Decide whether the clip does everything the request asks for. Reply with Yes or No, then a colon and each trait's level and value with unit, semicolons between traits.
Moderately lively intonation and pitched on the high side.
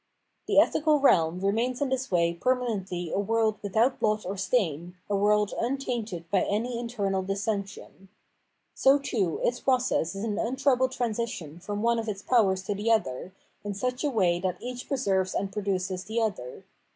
Yes: average, 4.3 semitones; high, 210 Hz